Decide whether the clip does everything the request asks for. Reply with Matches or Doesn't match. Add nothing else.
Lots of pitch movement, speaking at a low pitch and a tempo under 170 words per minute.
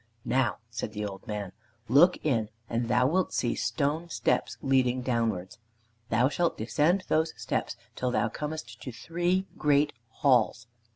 Doesn't match